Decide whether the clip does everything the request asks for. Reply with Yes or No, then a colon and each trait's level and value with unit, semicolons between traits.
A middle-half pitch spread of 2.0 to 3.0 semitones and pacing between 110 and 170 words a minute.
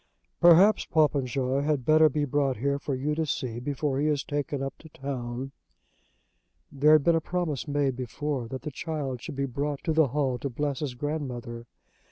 No: narrow, 2.5 semitones; average, 190 wpm